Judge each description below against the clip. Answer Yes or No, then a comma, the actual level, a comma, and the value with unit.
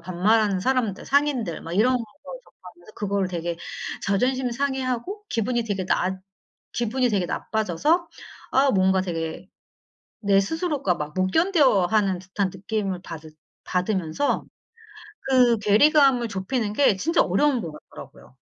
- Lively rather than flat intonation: Yes, wide, 5.7 semitones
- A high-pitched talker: Yes, high, 210 Hz